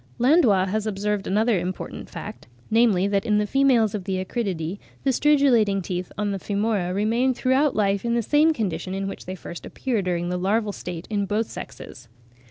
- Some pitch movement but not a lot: Yes, average, 3.8 semitones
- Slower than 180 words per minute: No, average, 185 wpm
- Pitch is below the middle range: No, high, 205 Hz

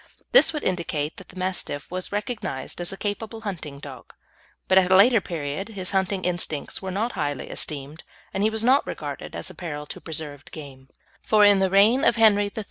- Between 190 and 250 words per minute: Yes, fast, 205 wpm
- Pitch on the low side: No, medium, 185 Hz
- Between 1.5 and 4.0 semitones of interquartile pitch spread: No, average, 5.3 semitones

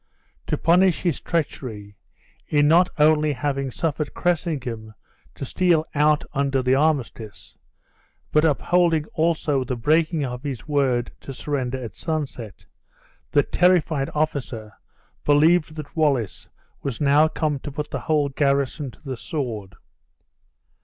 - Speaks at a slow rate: Yes, slow, 130 wpm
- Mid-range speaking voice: Yes, medium, 145 Hz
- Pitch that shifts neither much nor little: Yes, average, 3.2 semitones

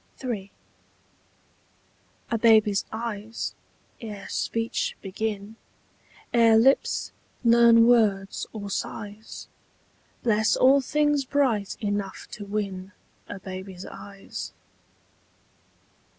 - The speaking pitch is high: Yes, high, 215 Hz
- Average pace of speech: No, slow, 85 wpm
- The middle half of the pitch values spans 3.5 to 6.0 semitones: No, narrow, 2.6 semitones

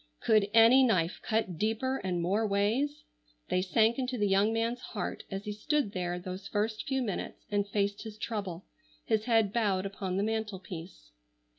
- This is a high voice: Yes, high, 210 Hz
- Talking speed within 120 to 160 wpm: No, average, 175 wpm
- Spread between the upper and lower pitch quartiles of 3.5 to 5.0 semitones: No, average, 2.7 semitones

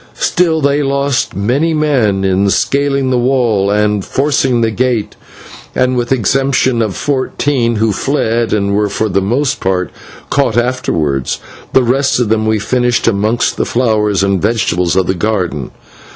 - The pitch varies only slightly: No, average, 4.7 semitones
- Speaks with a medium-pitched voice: No, low, 115 Hz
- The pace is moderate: Yes, average, 160 wpm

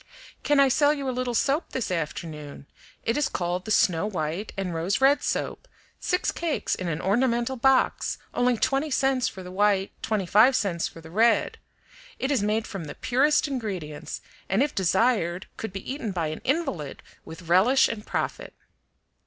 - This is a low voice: No, high, 215 Hz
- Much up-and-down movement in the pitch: Yes, wide, 6.6 semitones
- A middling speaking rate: Yes, average, 180 wpm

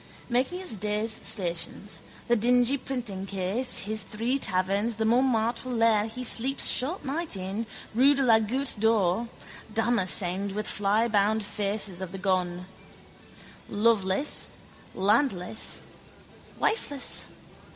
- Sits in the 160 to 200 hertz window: No, high, 220 Hz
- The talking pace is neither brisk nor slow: No, slow, 110 wpm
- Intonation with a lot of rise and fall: No, average, 3.7 semitones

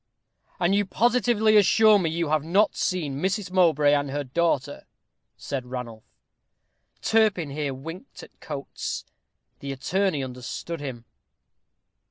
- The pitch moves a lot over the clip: Yes, wide, 5.9 semitones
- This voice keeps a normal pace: No, slow, 125 wpm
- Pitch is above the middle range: No, medium, 160 Hz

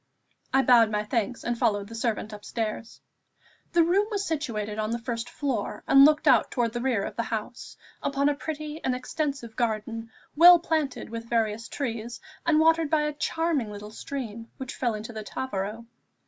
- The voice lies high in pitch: Yes, high, 240 Hz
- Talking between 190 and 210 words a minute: No, average, 180 wpm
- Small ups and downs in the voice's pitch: No, average, 4.8 semitones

